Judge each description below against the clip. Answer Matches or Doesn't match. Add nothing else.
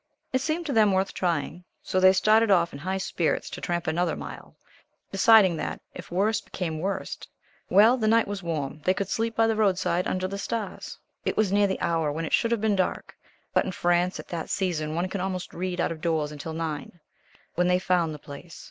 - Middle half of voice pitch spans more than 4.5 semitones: Doesn't match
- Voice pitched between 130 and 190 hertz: Matches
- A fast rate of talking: Matches